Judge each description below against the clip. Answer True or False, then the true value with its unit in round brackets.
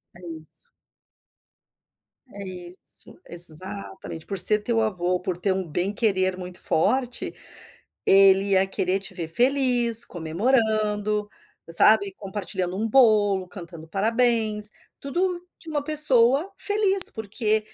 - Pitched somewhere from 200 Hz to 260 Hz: True (205 Hz)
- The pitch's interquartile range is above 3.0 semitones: True (4.2 semitones)